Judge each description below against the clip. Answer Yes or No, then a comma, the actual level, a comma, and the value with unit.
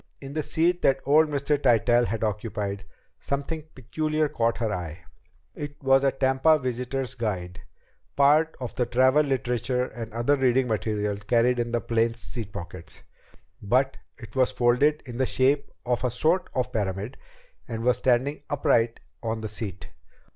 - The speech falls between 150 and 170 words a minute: Yes, average, 160 wpm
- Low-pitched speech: Yes, low, 125 Hz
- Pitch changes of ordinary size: Yes, average, 3.5 semitones